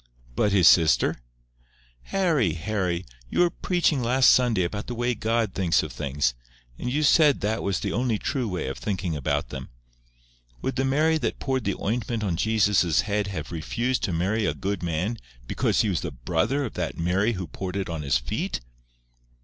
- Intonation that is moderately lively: No, wide, 6.0 semitones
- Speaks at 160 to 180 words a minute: No, average, 190 wpm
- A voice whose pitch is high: No, low, 105 Hz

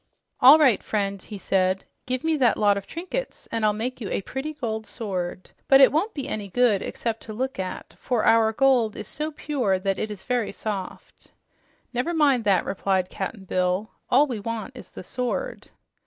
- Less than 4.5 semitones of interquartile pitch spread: No, average, 5.0 semitones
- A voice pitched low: No, high, 225 Hz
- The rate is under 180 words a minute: No, average, 195 wpm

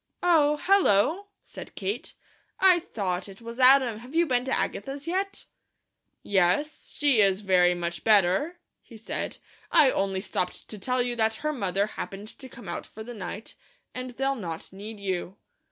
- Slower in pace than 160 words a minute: No, average, 170 wpm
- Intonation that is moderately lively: No, wide, 6.3 semitones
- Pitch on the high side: Yes, high, 225 Hz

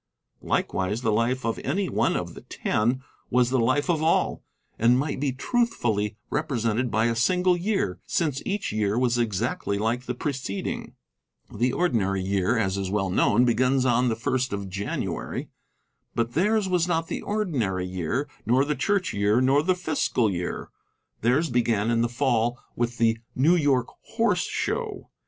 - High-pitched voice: No, low, 120 Hz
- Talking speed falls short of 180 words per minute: Yes, average, 165 wpm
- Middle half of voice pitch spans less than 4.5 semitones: No, average, 5.0 semitones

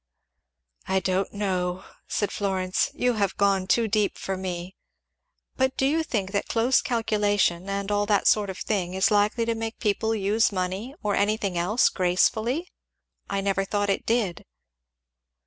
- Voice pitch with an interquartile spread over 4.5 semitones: No, average, 2.7 semitones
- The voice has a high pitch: Yes, high, 205 Hz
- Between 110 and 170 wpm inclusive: Yes, average, 160 wpm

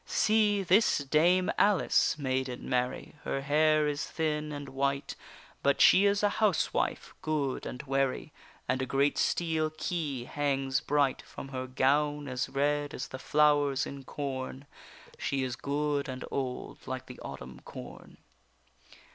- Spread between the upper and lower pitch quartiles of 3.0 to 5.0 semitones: No, narrow, 2.5 semitones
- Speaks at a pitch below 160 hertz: Yes, medium, 140 Hz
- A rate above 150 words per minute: No, average, 145 wpm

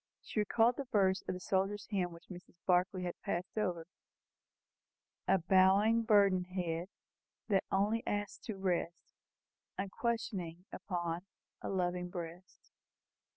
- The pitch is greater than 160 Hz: Yes, high, 190 Hz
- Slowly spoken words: Yes, slow, 125 wpm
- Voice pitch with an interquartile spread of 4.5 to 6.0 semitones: No, narrow, 2.5 semitones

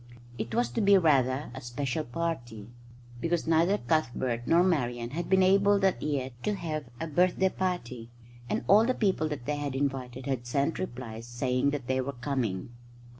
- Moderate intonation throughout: No, wide, 5.7 semitones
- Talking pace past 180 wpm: No, average, 175 wpm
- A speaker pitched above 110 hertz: Yes, medium, 140 Hz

